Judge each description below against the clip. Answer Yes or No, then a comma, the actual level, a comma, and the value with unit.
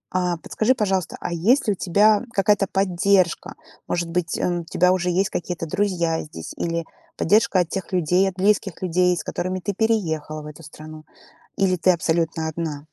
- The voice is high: No, medium, 180 Hz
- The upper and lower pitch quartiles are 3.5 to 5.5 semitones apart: No, average, 2.9 semitones